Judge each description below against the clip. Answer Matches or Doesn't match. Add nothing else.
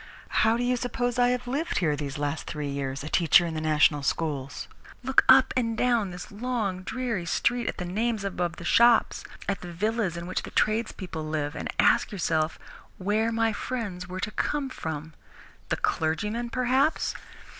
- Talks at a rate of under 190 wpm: Matches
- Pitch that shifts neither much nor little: Doesn't match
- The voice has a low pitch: Doesn't match